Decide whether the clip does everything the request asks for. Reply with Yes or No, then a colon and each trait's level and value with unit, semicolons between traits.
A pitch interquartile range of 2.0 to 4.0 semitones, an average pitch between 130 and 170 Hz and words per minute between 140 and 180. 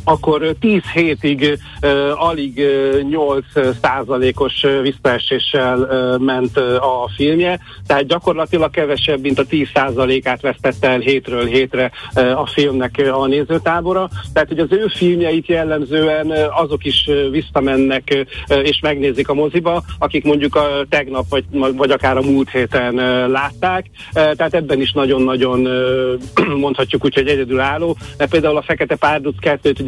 Yes: average, 2.8 semitones; medium, 140 Hz; fast, 155 wpm